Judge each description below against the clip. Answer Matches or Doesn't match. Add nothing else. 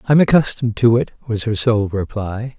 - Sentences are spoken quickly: Doesn't match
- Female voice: Doesn't match